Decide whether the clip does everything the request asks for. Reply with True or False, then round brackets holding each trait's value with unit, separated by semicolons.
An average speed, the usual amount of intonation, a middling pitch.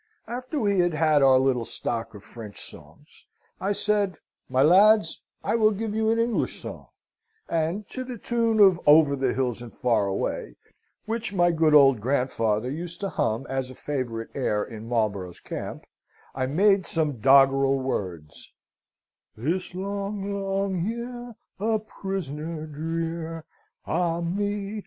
False (145 wpm; 7.6 semitones; 165 Hz)